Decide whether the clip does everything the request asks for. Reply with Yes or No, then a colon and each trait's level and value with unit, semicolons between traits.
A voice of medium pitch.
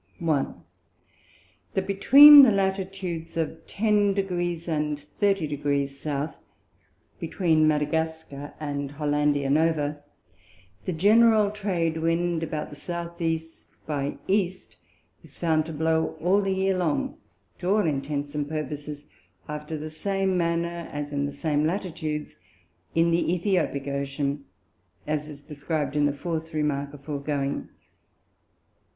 Yes: medium, 160 Hz